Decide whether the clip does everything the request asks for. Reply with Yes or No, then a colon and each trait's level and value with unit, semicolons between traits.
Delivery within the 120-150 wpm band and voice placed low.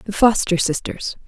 No: average, 140 wpm; high, 195 Hz